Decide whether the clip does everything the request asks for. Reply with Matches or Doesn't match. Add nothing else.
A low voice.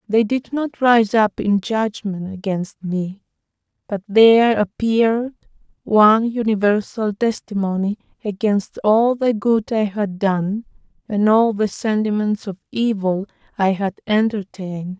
Doesn't match